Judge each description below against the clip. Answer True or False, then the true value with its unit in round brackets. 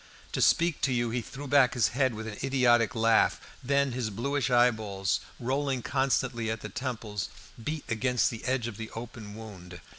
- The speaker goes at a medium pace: True (180 wpm)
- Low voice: True (120 Hz)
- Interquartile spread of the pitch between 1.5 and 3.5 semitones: True (3.0 semitones)